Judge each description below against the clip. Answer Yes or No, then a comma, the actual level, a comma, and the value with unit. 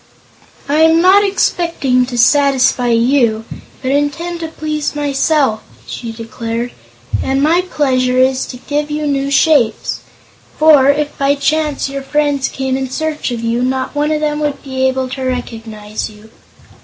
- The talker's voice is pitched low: No, very high, 275 Hz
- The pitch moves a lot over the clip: No, average, 3.1 semitones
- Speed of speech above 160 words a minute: No, average, 155 wpm